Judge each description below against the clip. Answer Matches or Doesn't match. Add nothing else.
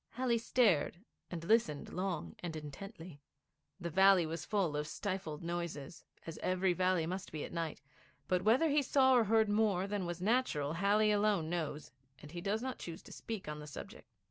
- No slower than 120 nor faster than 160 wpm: Doesn't match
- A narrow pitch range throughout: Doesn't match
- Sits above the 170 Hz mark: Matches